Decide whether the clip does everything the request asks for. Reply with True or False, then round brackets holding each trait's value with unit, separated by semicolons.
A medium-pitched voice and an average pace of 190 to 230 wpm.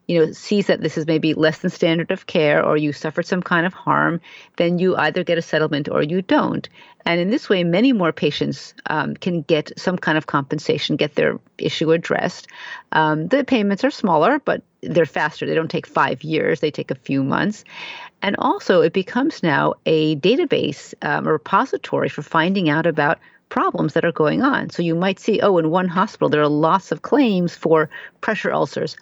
True (170 Hz; 205 wpm)